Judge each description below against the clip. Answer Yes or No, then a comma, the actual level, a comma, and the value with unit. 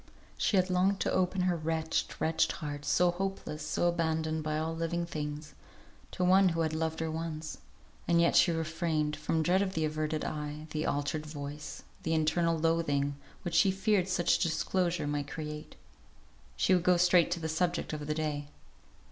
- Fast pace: No, average, 180 wpm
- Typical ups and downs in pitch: No, narrow, 2.3 semitones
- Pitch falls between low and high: Yes, medium, 160 Hz